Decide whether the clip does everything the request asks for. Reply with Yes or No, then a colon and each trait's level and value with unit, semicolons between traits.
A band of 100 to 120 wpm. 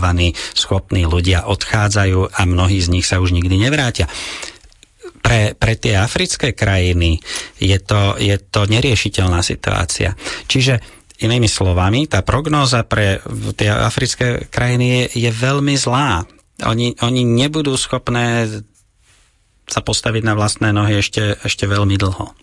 No: average, 130 wpm